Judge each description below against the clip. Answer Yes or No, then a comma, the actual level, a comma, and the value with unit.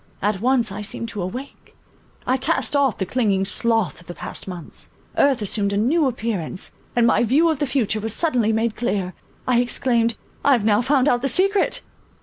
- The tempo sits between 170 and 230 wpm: Yes, average, 195 wpm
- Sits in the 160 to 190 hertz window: No, high, 235 Hz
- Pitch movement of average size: Yes, average, 4.2 semitones